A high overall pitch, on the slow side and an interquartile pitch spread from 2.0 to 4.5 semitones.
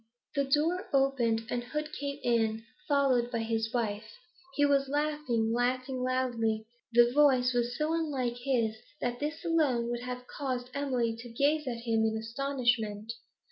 No: very high, 250 Hz; average, 155 wpm; average, 3.3 semitones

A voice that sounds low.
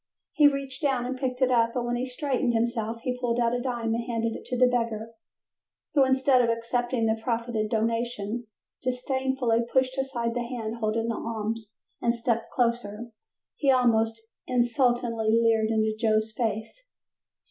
No: high, 235 Hz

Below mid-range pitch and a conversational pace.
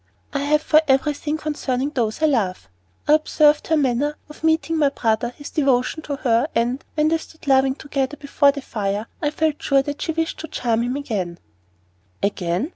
No: very high, 280 Hz; average, 190 wpm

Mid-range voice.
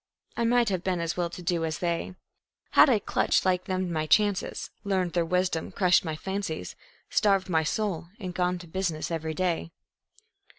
Yes: medium, 180 Hz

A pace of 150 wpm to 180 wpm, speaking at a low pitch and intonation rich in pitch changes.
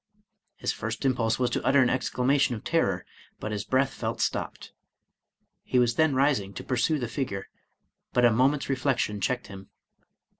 No: average, 165 wpm; low, 125 Hz; average, 3.8 semitones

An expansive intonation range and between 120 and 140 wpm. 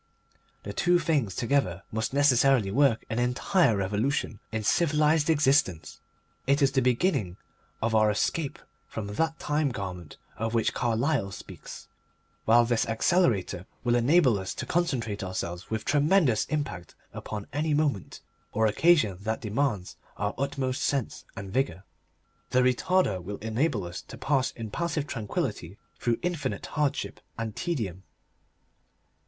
Yes: wide, 6.0 semitones; slow, 135 wpm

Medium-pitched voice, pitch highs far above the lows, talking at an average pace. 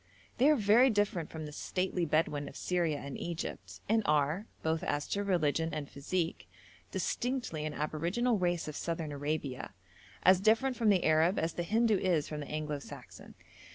No: medium, 165 Hz; average, 4.9 semitones; average, 175 wpm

